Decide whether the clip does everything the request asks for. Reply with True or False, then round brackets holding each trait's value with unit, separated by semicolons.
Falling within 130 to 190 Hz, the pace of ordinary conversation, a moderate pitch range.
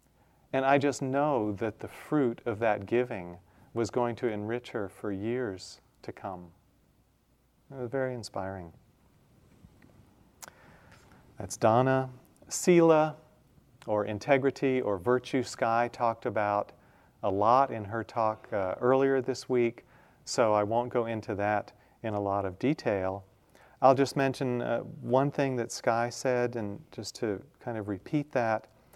False (115 Hz; 145 wpm; 4.1 semitones)